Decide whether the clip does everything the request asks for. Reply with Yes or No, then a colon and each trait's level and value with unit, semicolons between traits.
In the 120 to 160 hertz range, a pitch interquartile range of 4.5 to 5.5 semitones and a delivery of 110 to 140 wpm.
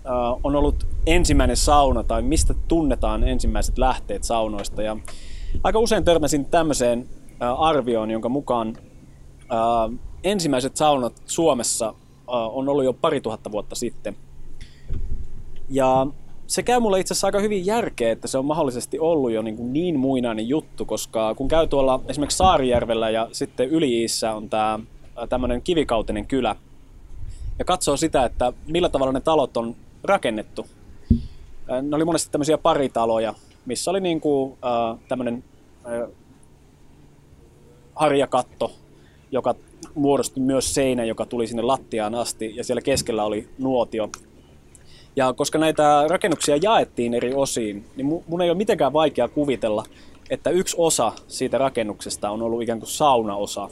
Yes: low, 125 Hz; average, 4.8 semitones; average, 135 wpm